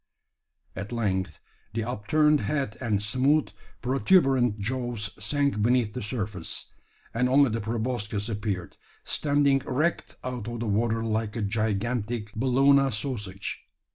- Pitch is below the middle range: Yes, low, 115 Hz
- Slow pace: Yes, slow, 125 wpm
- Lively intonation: No, average, 4.0 semitones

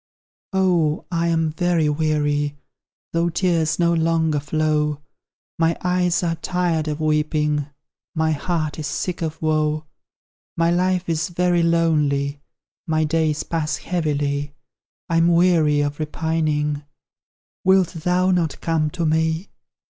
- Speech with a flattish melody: Yes, narrow, 2.1 semitones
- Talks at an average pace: No, slow, 125 wpm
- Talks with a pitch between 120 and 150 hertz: No, medium, 160 Hz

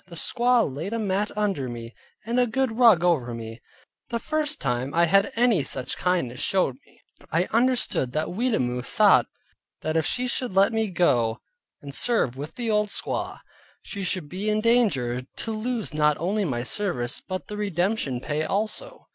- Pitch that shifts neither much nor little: No, wide, 8.3 semitones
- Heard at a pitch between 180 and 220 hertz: Yes, medium, 185 Hz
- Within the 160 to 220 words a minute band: Yes, average, 180 wpm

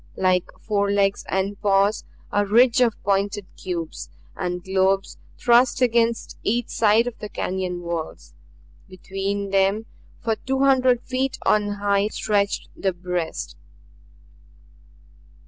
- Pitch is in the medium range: No, high, 200 Hz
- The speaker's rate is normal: No, slow, 115 wpm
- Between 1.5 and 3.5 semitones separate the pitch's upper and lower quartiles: Yes, average, 3.1 semitones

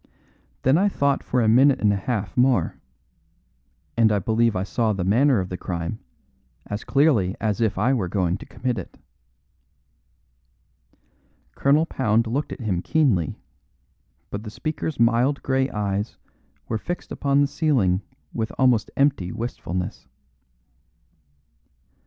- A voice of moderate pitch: No, low, 115 Hz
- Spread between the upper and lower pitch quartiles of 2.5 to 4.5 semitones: No, average, 5.2 semitones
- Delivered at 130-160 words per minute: Yes, average, 140 wpm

